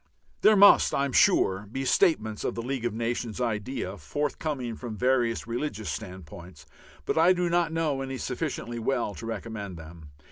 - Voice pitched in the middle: No, low, 120 Hz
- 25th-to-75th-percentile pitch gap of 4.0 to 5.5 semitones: Yes, average, 4.8 semitones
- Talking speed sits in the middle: Yes, average, 170 wpm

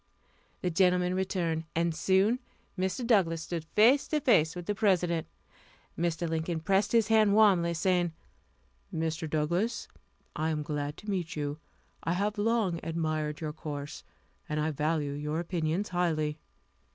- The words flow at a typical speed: Yes, average, 145 wpm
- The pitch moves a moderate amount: Yes, average, 3.5 semitones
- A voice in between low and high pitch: Yes, medium, 170 Hz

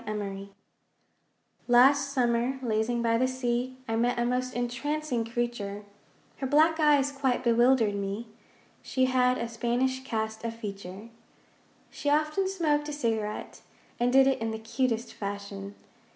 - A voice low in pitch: No, high, 240 Hz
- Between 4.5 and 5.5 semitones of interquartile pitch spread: No, average, 3.0 semitones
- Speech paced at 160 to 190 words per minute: No, average, 140 wpm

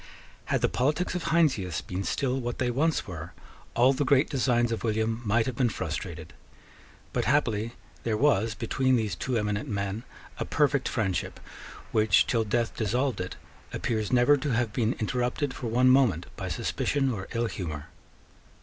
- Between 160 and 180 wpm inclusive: Yes, average, 170 wpm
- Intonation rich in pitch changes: No, average, 3.8 semitones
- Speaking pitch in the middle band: No, low, 120 Hz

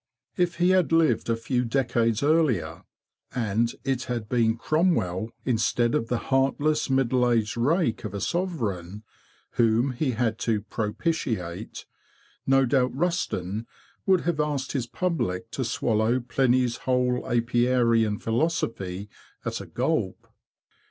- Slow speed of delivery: Yes, slow, 130 wpm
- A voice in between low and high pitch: No, low, 120 Hz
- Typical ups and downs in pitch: Yes, average, 3.5 semitones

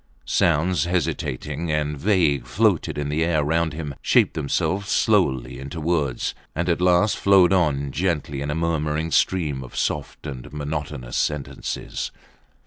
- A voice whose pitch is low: Yes, very low, 75 Hz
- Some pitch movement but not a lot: Yes, average, 3.2 semitones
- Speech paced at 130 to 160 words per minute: Yes, average, 140 wpm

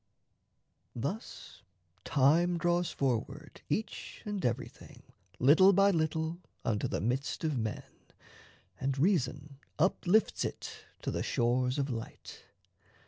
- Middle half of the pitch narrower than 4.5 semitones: No, average, 5.3 semitones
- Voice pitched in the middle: Yes, medium, 150 Hz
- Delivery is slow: Yes, slow, 110 wpm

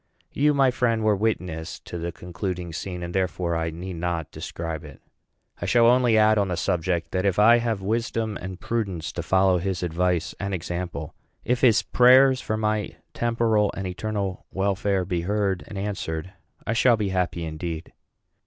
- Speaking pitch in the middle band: No, very low, 95 Hz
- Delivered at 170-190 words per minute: Yes, average, 175 wpm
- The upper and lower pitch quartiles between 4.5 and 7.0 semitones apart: No, average, 3.8 semitones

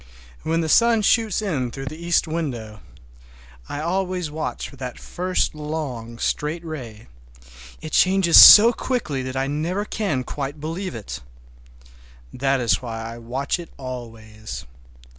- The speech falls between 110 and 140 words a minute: Yes, slow, 135 wpm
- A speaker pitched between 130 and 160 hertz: Yes, medium, 140 Hz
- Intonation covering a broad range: Yes, wide, 6.9 semitones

